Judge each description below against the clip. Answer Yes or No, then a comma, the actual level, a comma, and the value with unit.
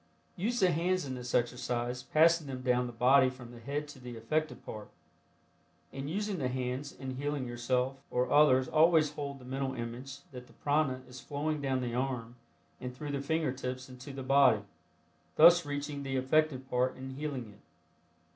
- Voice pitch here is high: No, low, 130 Hz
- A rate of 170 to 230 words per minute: Yes, average, 185 wpm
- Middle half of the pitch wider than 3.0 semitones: No, average, 2.7 semitones